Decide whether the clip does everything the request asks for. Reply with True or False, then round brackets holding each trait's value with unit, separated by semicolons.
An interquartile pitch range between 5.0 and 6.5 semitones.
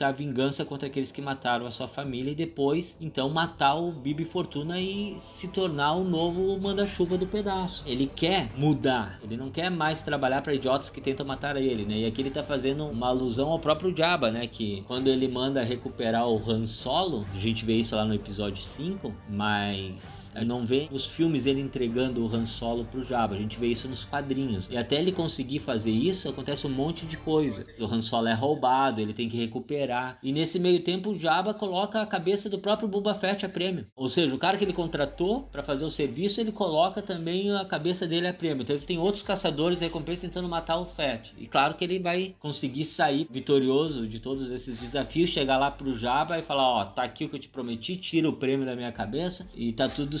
True (5.5 semitones)